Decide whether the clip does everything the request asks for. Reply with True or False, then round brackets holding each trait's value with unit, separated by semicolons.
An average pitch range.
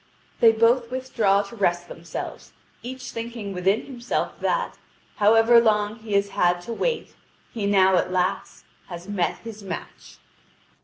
True (3.5 semitones)